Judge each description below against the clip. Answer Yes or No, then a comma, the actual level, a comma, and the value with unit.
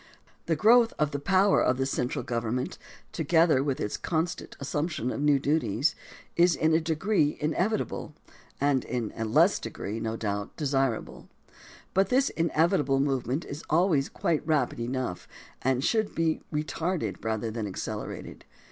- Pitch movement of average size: Yes, average, 4.8 semitones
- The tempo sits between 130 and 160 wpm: Yes, average, 150 wpm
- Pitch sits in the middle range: Yes, medium, 145 Hz